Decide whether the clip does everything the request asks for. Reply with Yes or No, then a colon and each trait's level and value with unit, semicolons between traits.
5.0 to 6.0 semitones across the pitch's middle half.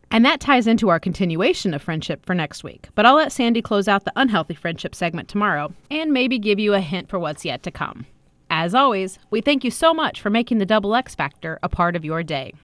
Yes: wide, 5.4 semitones